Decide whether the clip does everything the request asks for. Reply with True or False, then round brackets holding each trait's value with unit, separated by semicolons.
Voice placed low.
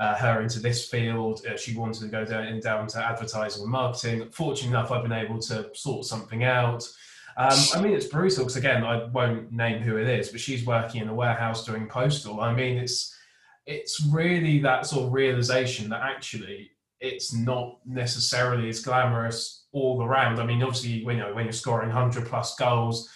True (120 Hz)